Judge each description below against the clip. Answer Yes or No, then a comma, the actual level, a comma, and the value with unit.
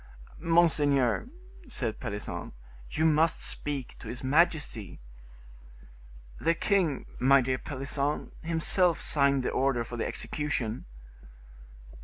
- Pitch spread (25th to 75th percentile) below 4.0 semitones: No, average, 4.3 semitones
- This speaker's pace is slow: Yes, slow, 105 wpm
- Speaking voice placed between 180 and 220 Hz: No, medium, 140 Hz